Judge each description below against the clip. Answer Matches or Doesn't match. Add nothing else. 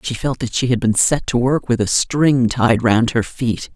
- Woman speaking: Matches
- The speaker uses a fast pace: Matches